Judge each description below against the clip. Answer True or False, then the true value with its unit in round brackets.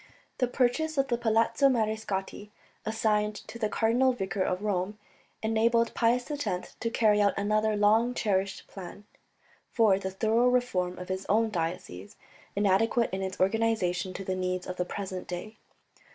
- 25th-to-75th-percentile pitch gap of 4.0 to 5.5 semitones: False (3.4 semitones)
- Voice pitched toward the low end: False (210 Hz)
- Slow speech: False (155 wpm)